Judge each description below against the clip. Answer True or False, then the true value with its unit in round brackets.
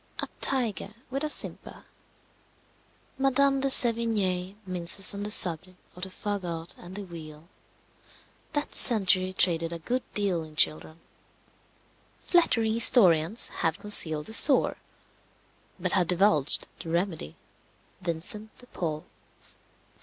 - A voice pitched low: False (185 Hz)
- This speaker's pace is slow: True (120 wpm)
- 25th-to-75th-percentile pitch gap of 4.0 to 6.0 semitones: True (4.8 semitones)